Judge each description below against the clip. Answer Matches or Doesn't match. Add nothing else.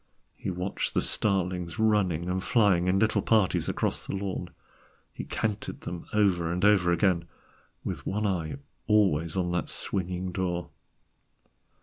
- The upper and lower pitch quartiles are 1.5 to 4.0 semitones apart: Matches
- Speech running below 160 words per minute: Matches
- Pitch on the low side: Matches